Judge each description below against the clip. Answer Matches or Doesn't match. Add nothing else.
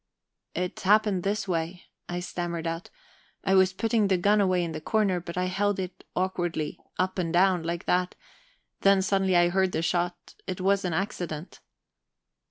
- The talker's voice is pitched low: Doesn't match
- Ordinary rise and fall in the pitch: Doesn't match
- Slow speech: Doesn't match